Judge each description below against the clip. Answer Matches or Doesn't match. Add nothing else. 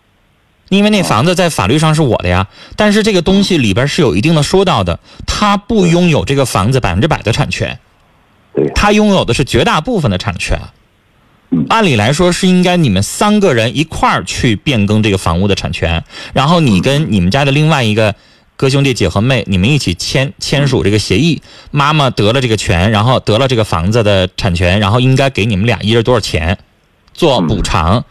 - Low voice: Matches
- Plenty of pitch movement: Matches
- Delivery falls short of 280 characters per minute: Doesn't match